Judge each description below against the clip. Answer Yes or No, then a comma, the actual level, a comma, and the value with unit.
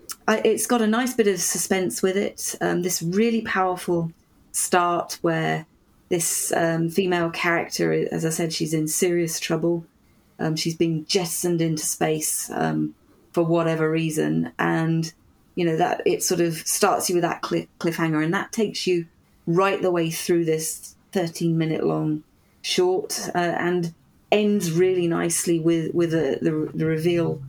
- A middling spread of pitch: No, narrow, 2.1 semitones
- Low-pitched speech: No, medium, 170 Hz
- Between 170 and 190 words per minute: No, average, 155 wpm